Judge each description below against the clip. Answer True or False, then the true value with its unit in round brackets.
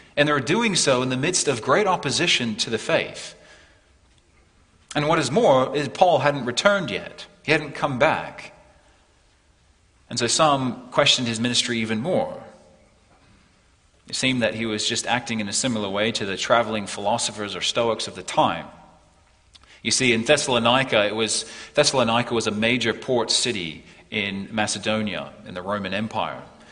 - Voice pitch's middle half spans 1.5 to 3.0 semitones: False (4.4 semitones)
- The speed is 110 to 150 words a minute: False (165 wpm)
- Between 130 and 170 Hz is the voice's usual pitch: False (115 Hz)